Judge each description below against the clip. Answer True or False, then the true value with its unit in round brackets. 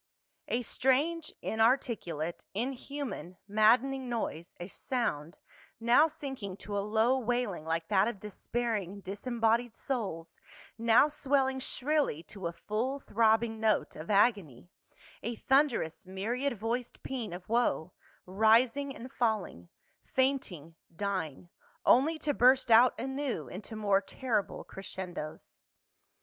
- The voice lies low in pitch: False (225 Hz)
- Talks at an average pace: False (120 wpm)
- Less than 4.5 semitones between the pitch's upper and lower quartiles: False (5.0 semitones)